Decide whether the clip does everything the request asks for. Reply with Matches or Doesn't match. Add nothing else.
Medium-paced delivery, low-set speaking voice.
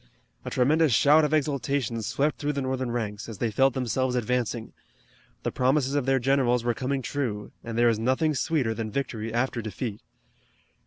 Matches